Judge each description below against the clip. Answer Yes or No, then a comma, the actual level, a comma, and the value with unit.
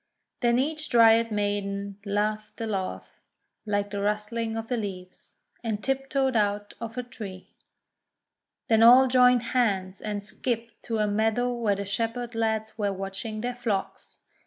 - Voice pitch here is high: Yes, high, 220 Hz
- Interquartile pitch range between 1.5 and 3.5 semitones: Yes, average, 2.8 semitones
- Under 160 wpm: Yes, average, 150 wpm